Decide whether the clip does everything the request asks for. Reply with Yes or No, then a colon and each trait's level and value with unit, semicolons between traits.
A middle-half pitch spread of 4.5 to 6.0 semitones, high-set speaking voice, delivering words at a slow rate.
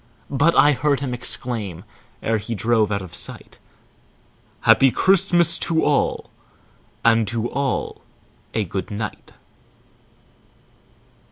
No: average, 5.1 semitones; low, 120 Hz; slow, 110 wpm